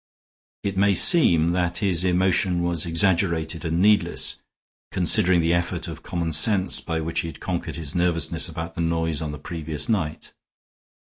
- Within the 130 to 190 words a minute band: Yes, average, 165 wpm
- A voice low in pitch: Yes, very low, 85 Hz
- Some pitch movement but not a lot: No, narrow, 2.1 semitones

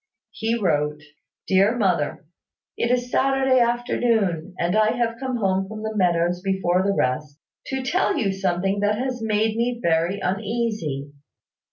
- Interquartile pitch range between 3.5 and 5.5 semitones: Yes, average, 4.9 semitones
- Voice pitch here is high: Yes, high, 205 Hz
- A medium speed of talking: Yes, average, 150 wpm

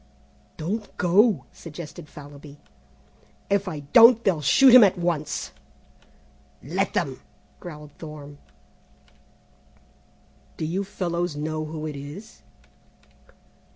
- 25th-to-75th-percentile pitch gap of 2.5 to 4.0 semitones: No, average, 4.6 semitones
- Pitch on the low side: No, medium, 160 Hz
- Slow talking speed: Yes, slow, 100 wpm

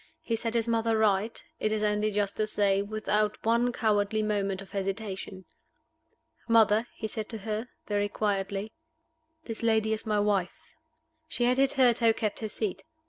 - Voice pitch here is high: Yes, high, 215 Hz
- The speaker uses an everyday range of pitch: No, narrow, 1.7 semitones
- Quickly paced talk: No, average, 160 wpm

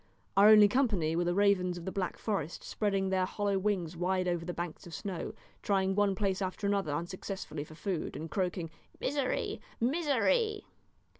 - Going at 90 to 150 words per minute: No, average, 170 wpm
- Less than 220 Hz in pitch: Yes, high, 190 Hz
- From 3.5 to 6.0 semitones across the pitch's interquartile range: No, average, 2.8 semitones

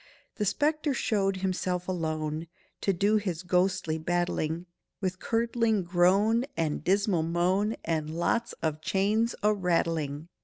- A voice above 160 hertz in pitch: Yes, medium, 185 Hz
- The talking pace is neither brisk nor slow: No, slow, 125 wpm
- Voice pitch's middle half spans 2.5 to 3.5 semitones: No, average, 3.9 semitones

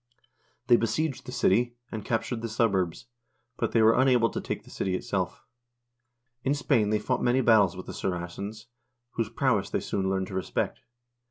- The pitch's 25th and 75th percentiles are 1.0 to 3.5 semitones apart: No, average, 4.0 semitones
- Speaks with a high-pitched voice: No, low, 110 Hz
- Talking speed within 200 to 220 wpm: No, average, 175 wpm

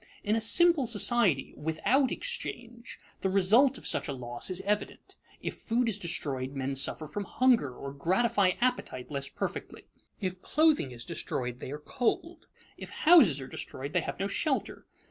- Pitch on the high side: Yes, high, 195 Hz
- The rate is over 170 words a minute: No, average, 165 wpm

